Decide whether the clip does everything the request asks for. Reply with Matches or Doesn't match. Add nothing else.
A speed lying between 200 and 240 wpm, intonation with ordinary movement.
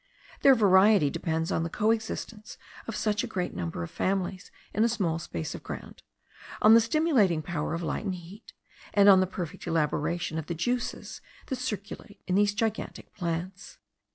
Doesn't match